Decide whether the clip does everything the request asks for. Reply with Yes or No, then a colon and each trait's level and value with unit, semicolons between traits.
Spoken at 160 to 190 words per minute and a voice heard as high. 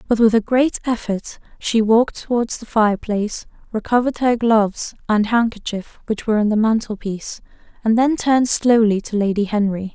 Yes: average, 170 wpm; high, 220 Hz